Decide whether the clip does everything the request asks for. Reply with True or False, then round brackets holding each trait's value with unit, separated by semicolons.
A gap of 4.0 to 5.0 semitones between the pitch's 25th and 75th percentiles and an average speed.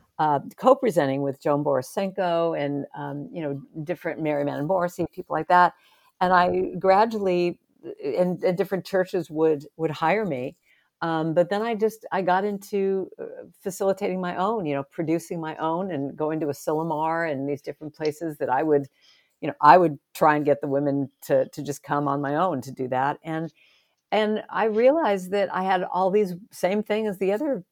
True (4.7 semitones; 190 wpm)